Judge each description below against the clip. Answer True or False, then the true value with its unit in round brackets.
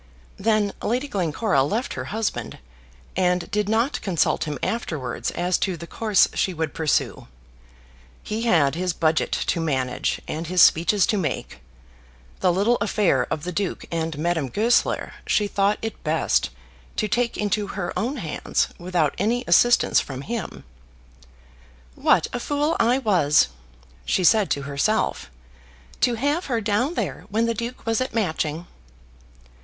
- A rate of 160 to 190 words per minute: False (150 wpm)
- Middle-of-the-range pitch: False (195 Hz)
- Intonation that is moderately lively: False (5.7 semitones)